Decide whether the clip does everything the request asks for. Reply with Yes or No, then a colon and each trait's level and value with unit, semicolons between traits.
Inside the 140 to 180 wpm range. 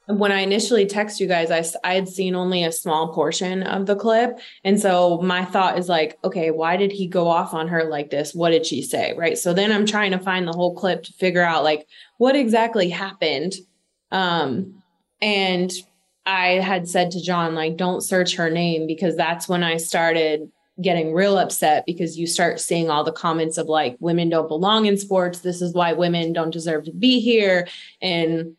No: fast, 205 wpm